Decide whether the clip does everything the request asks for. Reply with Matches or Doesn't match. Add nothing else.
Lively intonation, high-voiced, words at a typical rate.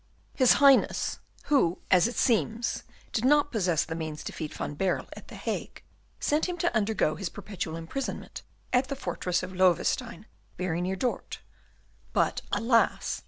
Matches